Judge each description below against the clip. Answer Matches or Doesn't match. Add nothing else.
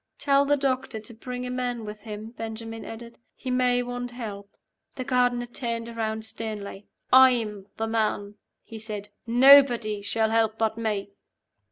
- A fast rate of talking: Doesn't match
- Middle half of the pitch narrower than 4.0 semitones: Matches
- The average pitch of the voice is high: Matches